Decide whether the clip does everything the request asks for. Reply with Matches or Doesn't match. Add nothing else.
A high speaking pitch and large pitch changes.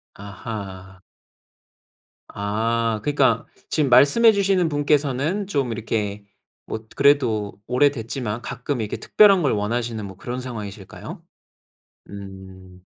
Doesn't match